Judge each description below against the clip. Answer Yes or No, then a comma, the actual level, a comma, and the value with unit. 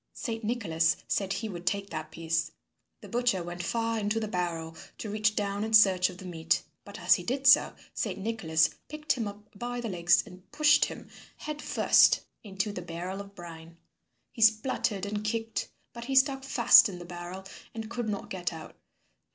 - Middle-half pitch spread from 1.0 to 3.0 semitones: No, average, 4.4 semitones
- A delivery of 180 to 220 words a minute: Yes, average, 190 wpm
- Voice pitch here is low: No, high, 200 Hz